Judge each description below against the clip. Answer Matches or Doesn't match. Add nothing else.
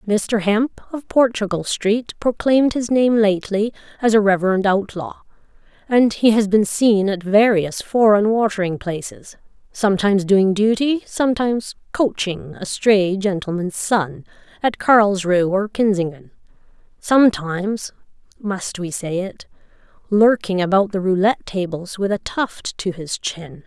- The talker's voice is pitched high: Matches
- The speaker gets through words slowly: Matches